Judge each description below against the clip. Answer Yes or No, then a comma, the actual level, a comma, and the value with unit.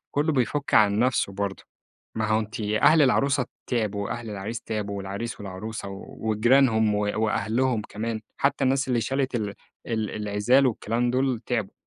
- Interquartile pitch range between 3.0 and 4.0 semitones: Yes, average, 3.5 semitones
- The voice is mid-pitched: No, low, 110 Hz